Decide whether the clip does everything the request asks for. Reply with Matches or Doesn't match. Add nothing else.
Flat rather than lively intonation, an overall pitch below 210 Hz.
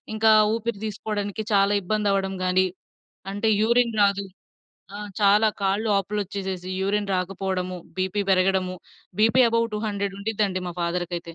Matches